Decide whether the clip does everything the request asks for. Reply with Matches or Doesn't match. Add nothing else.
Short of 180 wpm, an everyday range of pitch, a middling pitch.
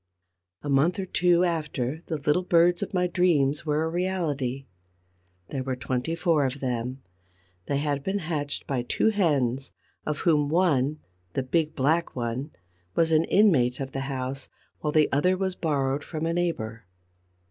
Matches